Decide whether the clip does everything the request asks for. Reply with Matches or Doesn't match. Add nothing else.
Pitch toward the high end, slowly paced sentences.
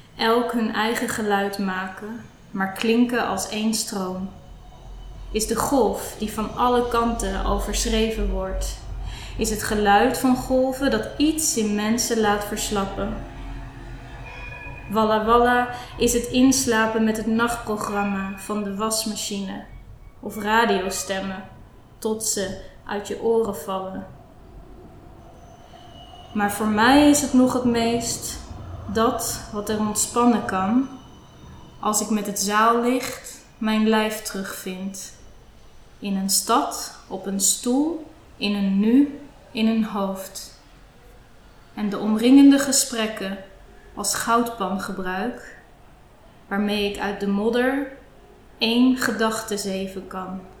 Matches